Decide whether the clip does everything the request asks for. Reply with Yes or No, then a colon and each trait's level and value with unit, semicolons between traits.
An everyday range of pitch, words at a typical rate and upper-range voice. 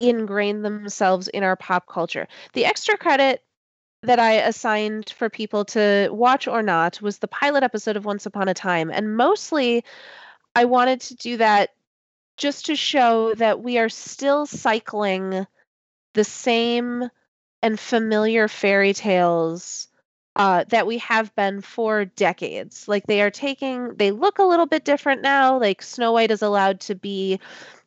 Yes: average, 3.5 semitones; average, 155 wpm; high, 220 Hz